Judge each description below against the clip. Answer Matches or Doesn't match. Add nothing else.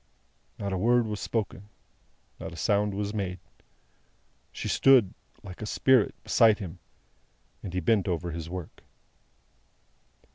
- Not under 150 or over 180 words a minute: Doesn't match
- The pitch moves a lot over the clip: Doesn't match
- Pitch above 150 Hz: Doesn't match